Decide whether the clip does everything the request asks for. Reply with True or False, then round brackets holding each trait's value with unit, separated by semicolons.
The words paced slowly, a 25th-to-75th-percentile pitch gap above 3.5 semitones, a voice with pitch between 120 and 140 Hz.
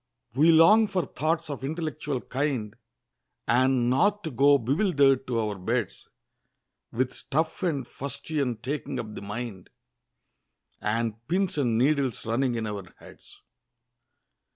True (130 wpm; 4.8 semitones; 135 Hz)